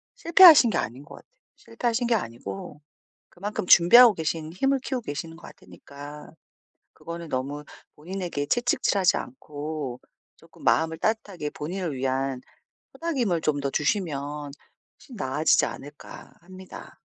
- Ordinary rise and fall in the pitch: No, wide, 6.3 semitones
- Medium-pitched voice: Yes, medium, 160 Hz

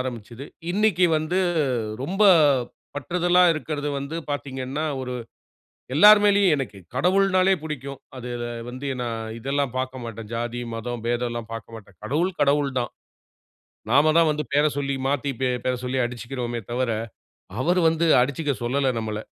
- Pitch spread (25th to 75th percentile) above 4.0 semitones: Yes, average, 4.4 semitones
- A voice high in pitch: No, low, 135 Hz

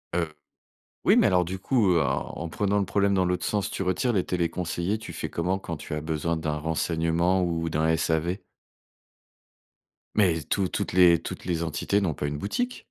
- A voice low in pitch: Yes, very low, 85 Hz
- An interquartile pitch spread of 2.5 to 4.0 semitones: Yes, average, 2.8 semitones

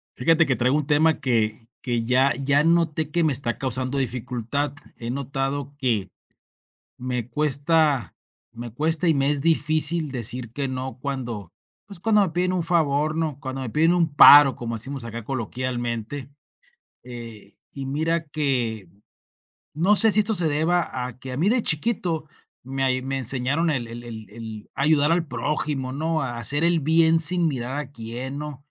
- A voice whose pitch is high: No, medium, 140 Hz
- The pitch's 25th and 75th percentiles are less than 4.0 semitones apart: No, average, 4.3 semitones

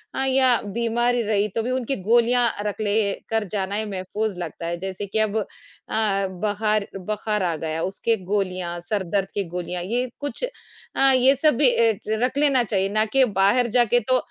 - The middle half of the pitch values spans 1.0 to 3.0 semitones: No, average, 3.8 semitones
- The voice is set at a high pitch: Yes, high, 215 Hz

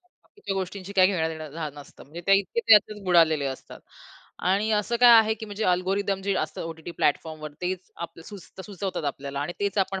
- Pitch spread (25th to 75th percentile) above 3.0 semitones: Yes, average, 3.9 semitones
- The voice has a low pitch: No, medium, 185 Hz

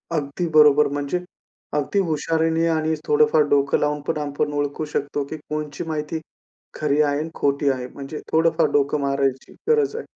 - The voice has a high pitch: No, medium, 150 Hz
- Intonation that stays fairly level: Yes, narrow, 1.9 semitones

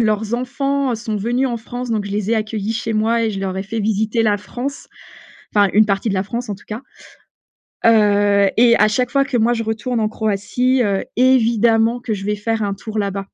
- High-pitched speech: Yes, high, 220 Hz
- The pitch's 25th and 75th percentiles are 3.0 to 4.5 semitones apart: No, narrow, 2.5 semitones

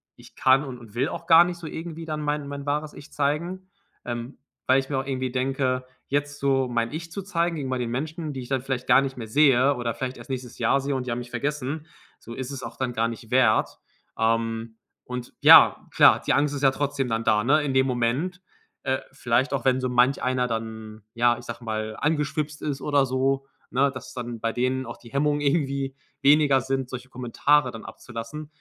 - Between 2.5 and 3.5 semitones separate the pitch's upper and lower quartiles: Yes, average, 2.9 semitones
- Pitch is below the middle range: Yes, low, 130 Hz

